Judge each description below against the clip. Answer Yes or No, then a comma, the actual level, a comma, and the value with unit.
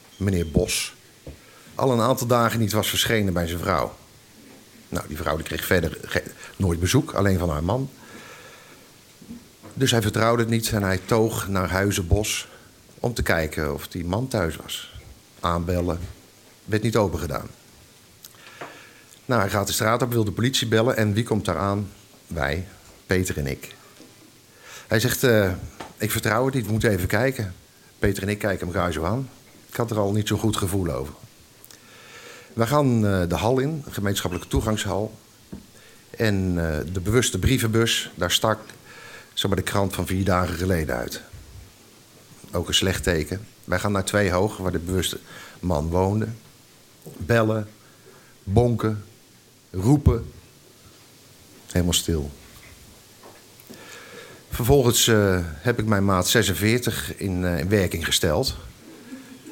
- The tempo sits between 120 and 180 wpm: Yes, average, 150 wpm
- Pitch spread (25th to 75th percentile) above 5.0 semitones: No, average, 4.0 semitones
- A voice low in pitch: Yes, low, 100 Hz